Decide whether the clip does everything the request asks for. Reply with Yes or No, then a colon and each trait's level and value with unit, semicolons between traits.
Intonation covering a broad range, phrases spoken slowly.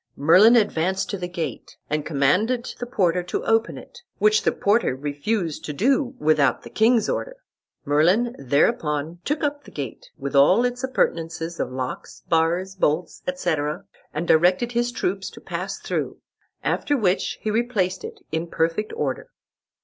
No: wide, 6.8 semitones; average, 155 wpm